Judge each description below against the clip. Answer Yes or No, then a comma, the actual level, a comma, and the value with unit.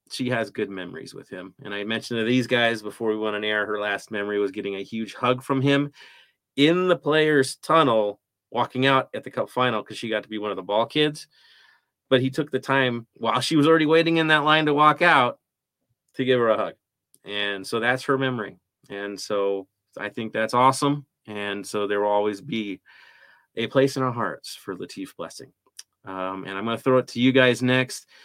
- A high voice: No, low, 120 Hz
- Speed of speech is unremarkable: No, fast, 220 wpm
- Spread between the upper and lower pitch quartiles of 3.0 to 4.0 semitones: No, average, 4.6 semitones